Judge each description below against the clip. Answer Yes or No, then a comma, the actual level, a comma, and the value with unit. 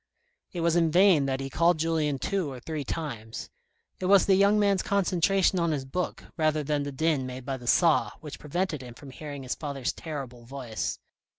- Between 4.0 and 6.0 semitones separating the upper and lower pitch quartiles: Yes, average, 4.4 semitones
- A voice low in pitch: No, medium, 155 Hz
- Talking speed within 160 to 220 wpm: Yes, average, 200 wpm